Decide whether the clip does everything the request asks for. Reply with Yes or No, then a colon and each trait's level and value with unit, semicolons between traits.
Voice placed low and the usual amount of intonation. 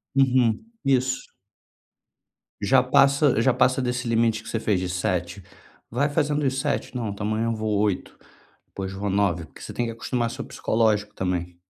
Yes: low, 115 Hz; average, 4.2 semitones